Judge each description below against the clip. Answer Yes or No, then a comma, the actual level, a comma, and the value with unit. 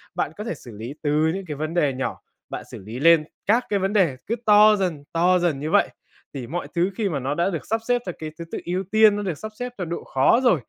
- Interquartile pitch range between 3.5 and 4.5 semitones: No, wide, 5.5 semitones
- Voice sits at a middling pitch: Yes, medium, 175 Hz